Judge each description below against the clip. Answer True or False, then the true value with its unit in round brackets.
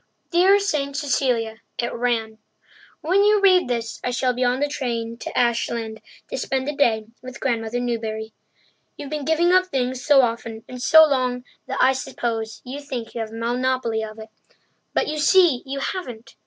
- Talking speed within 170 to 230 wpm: True (180 wpm)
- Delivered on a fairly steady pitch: False (3.9 semitones)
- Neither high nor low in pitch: False (250 Hz)